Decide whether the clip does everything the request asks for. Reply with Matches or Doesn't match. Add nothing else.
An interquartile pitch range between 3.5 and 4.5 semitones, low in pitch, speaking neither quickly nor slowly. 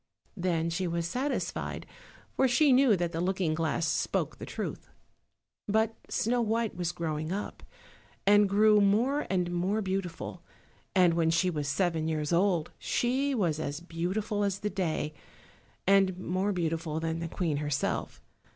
Doesn't match